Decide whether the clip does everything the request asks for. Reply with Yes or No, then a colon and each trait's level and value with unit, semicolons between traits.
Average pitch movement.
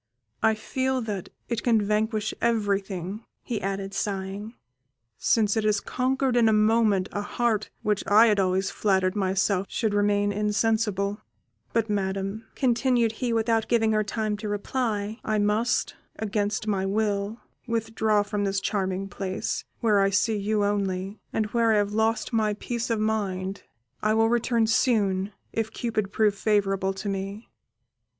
No: narrow, 2.1 semitones